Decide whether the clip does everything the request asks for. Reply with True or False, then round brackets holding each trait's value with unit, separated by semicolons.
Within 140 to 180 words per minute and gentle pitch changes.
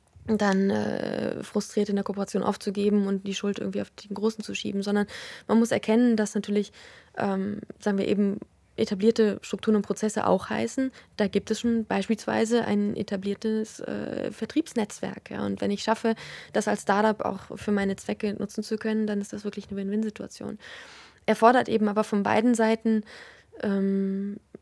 True (170 wpm; 1.6 semitones)